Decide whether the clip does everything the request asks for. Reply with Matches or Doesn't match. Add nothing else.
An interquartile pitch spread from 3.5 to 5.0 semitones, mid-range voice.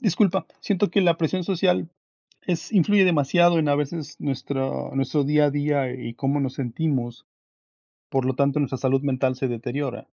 Matches